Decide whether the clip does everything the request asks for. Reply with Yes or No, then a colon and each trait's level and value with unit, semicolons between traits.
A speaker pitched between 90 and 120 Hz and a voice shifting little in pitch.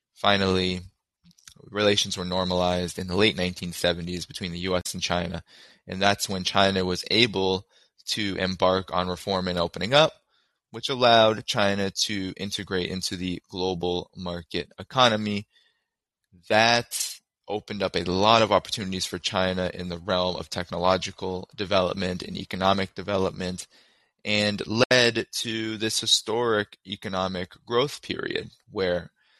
Yes: very low, 95 Hz; narrow, 2.3 semitones